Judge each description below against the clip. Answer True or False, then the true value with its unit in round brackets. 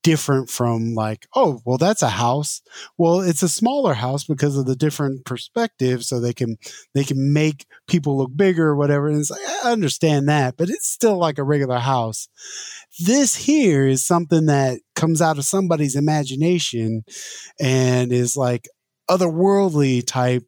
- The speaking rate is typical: True (165 wpm)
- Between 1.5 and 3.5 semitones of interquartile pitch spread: False (4.8 semitones)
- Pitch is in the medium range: True (145 Hz)